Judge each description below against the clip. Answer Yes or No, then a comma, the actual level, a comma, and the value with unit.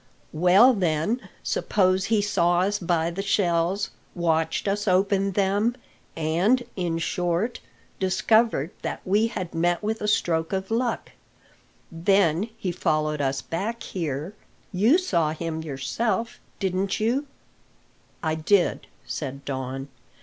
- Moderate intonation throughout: Yes, average, 4.1 semitones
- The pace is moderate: No, slow, 125 wpm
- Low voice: No, medium, 185 Hz